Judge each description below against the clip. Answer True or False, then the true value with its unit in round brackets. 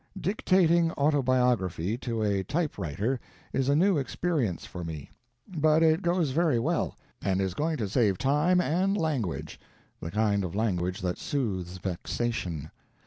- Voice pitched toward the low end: True (125 Hz)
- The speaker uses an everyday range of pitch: False (9.0 semitones)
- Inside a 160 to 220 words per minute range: False (140 wpm)